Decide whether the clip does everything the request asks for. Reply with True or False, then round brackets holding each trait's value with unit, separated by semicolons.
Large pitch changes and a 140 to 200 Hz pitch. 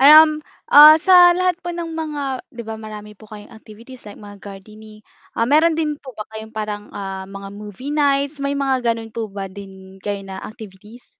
False (5.9 semitones; 220 Hz)